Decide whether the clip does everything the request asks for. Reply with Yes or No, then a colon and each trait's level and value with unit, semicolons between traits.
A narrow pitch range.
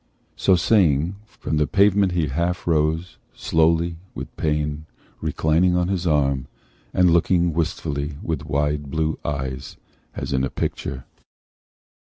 No: average, 3.1 semitones